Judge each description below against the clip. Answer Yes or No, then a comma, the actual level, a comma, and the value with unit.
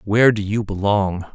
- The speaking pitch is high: No, low, 100 Hz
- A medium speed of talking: Yes, average, 180 wpm